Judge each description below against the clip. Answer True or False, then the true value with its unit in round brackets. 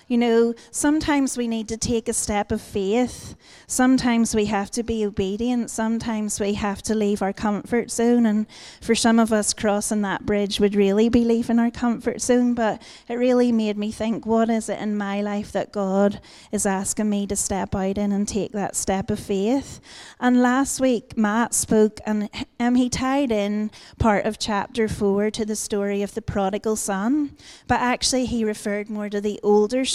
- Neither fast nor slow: True (190 wpm)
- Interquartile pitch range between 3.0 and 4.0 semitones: False (2.5 semitones)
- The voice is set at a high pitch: True (220 Hz)